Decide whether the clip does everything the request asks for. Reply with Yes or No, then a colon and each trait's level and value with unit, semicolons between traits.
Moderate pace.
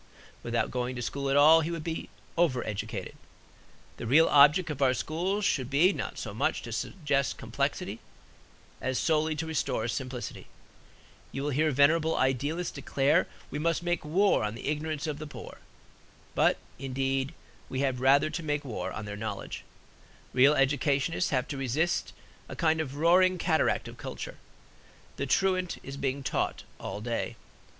Yes: average, 165 wpm